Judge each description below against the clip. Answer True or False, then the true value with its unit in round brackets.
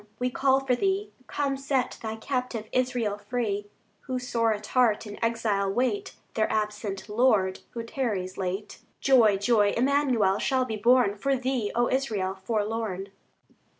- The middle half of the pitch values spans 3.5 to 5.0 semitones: True (3.8 semitones)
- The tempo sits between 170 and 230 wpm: False (150 wpm)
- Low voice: False (230 Hz)